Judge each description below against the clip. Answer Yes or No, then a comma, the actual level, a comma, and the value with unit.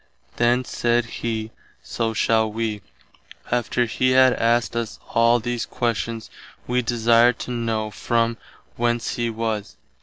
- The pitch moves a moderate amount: No, narrow, 1.1 semitones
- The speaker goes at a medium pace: No, slow, 130 wpm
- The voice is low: Yes, low, 115 Hz